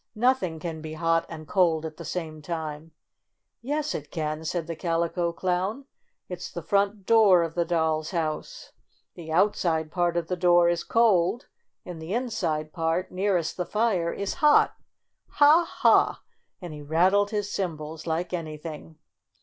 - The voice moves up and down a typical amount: Yes, average, 3.4 semitones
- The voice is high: No, medium, 170 Hz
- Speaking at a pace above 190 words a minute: No, average, 165 wpm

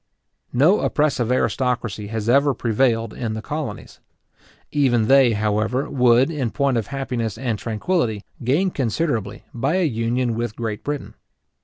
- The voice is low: Yes, low, 120 Hz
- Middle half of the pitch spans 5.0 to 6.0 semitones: No, average, 3.7 semitones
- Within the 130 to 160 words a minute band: Yes, average, 140 wpm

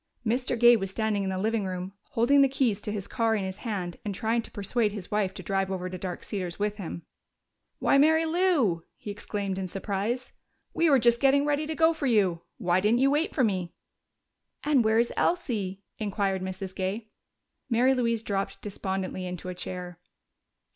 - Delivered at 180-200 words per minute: Yes, average, 195 wpm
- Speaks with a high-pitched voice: Yes, high, 210 Hz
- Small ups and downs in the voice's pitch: No, average, 4.3 semitones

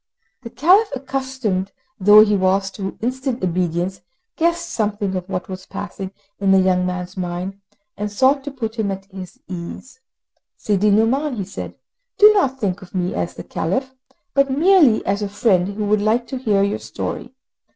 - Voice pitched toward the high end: Yes, high, 205 Hz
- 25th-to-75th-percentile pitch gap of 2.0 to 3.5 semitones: No, wide, 5.6 semitones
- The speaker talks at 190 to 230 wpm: No, average, 175 wpm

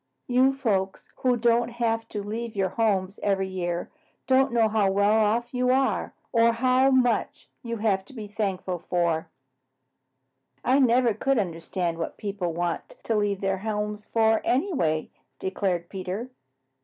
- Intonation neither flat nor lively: Yes, average, 3.9 semitones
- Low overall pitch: No, high, 215 Hz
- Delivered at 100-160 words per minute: Yes, average, 150 wpm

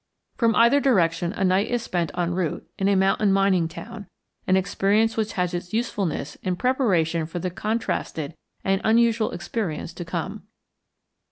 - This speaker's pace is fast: No, average, 160 wpm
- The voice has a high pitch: Yes, high, 195 Hz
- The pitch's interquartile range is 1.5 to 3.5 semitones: No, average, 4.1 semitones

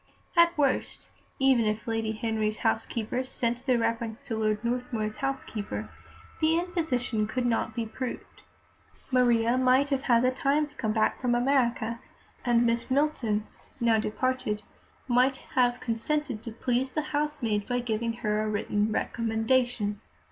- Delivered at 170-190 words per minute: No, average, 140 wpm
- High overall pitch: Yes, high, 240 Hz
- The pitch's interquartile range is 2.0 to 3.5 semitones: Yes, average, 2.7 semitones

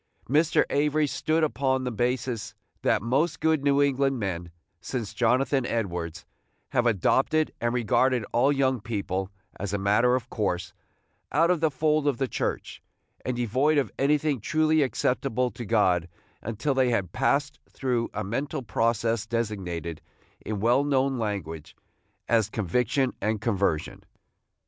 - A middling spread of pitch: Yes, average, 4.6 semitones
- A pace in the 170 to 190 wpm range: No, average, 145 wpm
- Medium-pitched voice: No, low, 120 Hz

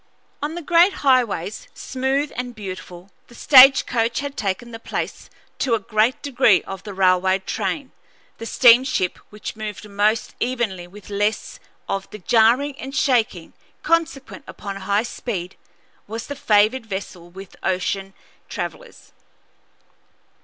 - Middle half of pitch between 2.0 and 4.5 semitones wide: No, average, 4.9 semitones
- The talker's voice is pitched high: Yes, high, 220 Hz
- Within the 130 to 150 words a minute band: Yes, average, 140 wpm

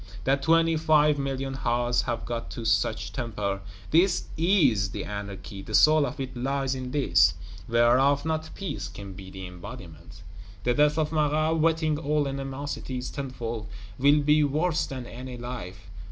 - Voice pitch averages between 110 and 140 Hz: Yes, low, 135 Hz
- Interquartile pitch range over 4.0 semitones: Yes, average, 4.7 semitones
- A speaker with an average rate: Yes, average, 155 wpm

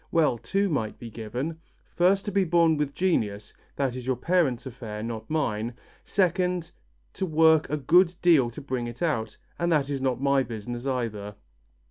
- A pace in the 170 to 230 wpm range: Yes, average, 175 wpm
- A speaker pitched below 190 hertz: Yes, medium, 140 Hz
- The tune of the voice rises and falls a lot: Yes, wide, 6.0 semitones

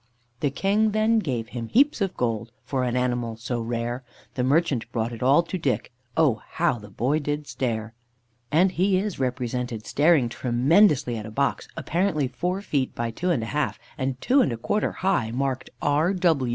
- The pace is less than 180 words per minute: No, average, 185 wpm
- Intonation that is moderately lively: No, wide, 6.2 semitones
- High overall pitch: No, low, 130 Hz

